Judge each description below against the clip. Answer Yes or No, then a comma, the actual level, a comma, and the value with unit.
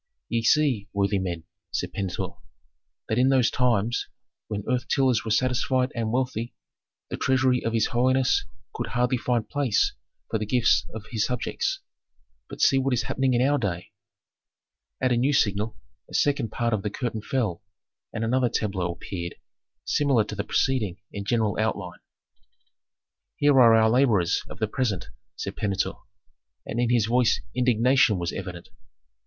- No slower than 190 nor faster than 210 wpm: No, average, 160 wpm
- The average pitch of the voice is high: No, low, 115 Hz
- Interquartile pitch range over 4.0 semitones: No, average, 3.5 semitones